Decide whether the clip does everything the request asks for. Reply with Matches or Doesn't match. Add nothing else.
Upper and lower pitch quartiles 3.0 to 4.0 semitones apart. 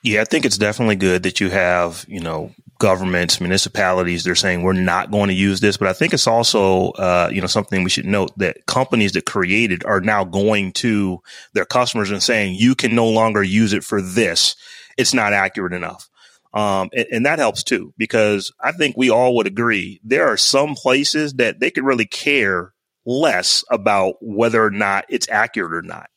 Matches